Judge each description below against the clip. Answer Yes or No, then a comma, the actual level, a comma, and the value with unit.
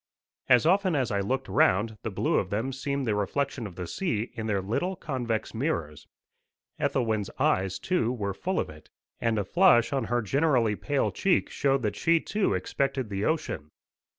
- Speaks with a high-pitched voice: No, low, 120 Hz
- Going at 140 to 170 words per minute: No, average, 180 wpm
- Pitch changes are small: No, wide, 5.5 semitones